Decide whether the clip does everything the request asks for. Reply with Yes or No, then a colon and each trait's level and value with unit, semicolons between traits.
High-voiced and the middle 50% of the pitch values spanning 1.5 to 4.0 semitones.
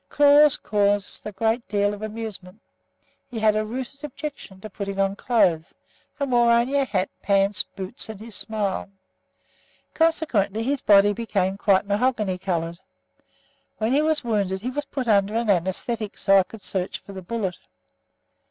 Yes: high, 210 Hz; average, 3.4 semitones